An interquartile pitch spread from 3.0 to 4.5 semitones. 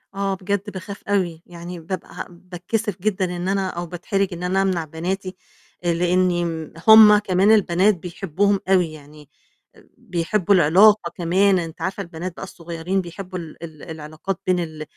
No: narrow, 2.5 semitones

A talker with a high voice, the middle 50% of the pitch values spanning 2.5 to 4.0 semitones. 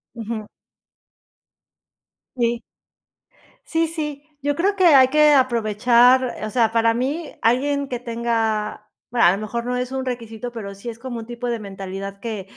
Yes: high, 235 Hz; average, 2.9 semitones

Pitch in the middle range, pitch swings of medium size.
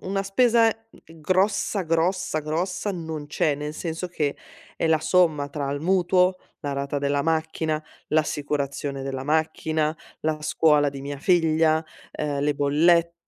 Yes: medium, 155 Hz; average, 3.1 semitones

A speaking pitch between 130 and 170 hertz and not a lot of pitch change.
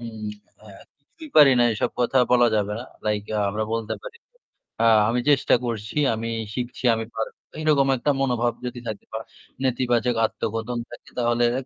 No: low, 120 Hz; narrow, 2.3 semitones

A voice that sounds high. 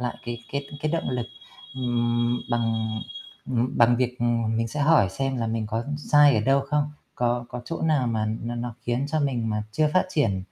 No: low, 120 Hz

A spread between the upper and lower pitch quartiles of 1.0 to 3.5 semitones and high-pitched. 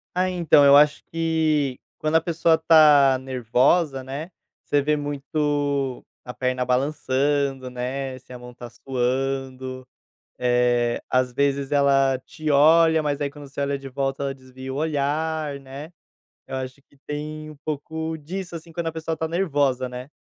No: average, 2.9 semitones; medium, 140 Hz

